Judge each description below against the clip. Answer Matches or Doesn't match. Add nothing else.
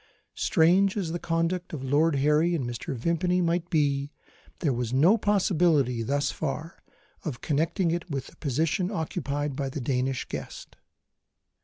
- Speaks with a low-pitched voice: Doesn't match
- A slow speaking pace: Doesn't match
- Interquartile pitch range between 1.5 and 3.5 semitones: Doesn't match